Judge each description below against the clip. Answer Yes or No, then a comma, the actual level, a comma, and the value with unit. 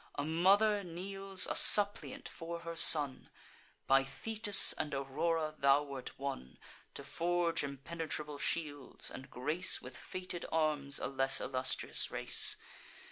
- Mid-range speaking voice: Yes, medium, 155 Hz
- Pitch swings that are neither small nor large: Yes, average, 4.1 semitones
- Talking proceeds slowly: Yes, slow, 130 wpm